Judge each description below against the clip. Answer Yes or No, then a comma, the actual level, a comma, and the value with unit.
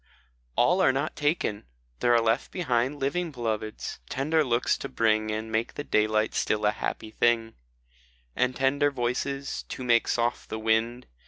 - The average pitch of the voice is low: Yes, low, 120 Hz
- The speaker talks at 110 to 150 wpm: No, average, 165 wpm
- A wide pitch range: No, average, 3.6 semitones